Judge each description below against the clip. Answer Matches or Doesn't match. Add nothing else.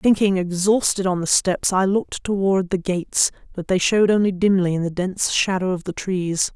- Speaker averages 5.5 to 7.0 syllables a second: Doesn't match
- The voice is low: Doesn't match